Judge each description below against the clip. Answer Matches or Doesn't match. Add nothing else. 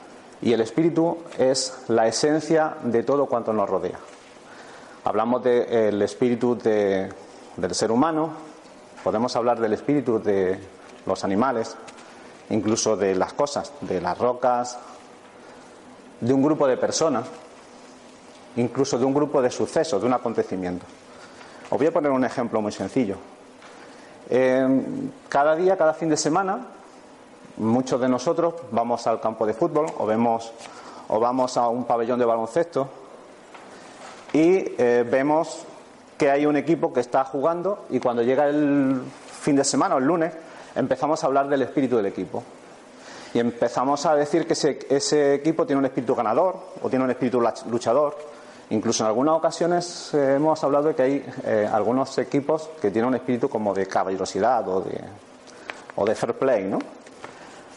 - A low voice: Matches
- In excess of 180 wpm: Doesn't match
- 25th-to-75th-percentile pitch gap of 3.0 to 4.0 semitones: Doesn't match